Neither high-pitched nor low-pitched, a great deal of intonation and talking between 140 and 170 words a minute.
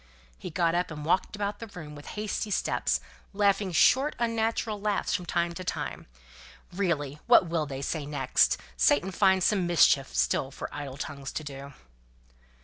Yes: medium, 170 Hz; wide, 5.7 semitones; average, 165 wpm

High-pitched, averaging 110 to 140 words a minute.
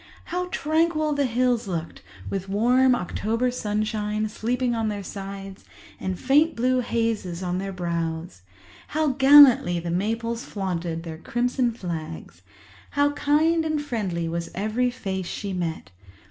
Yes: high, 215 Hz; slow, 135 wpm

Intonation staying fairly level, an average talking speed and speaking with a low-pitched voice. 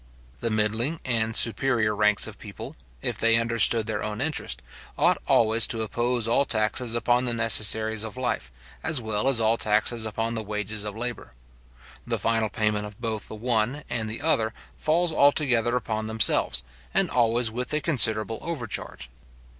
Yes: narrow, 2.1 semitones; average, 165 wpm; low, 115 Hz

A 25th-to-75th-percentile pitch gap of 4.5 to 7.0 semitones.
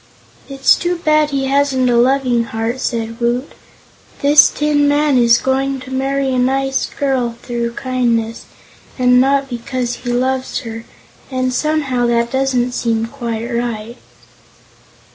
No: narrow, 2.4 semitones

